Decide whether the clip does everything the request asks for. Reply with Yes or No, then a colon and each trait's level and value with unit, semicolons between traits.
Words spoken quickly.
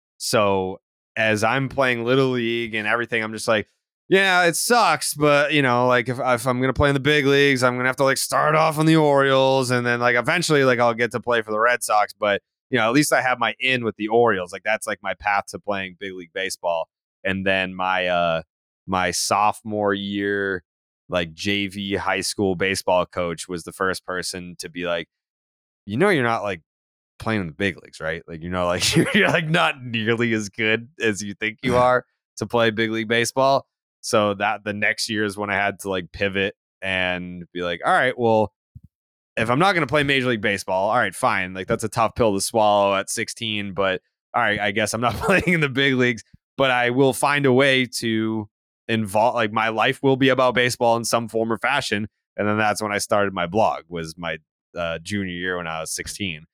Yes: fast, 225 wpm